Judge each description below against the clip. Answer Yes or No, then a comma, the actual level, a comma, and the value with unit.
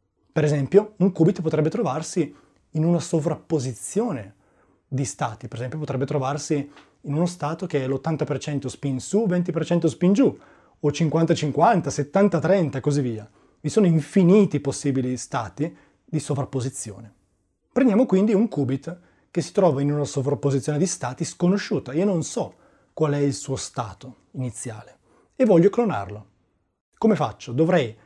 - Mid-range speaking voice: Yes, medium, 150 Hz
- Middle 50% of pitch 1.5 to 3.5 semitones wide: No, average, 4.7 semitones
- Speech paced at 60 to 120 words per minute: No, average, 145 wpm